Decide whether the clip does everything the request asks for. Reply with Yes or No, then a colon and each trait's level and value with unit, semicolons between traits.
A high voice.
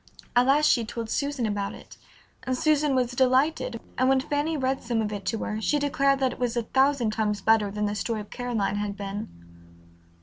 Yes: high, 245 Hz